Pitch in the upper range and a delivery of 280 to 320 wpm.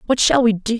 Yes: high, 230 Hz; fast, 305 wpm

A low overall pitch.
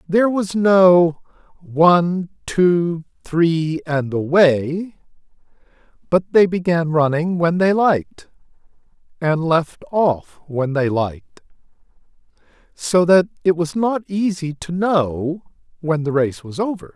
No: medium, 165 Hz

